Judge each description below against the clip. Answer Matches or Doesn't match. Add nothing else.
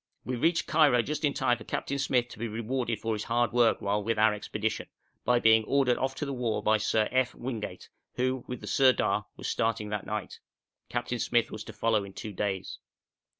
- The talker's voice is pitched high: Doesn't match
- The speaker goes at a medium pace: Doesn't match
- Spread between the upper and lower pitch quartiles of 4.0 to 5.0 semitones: Doesn't match